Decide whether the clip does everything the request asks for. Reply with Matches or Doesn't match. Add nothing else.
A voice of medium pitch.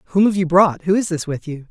Matches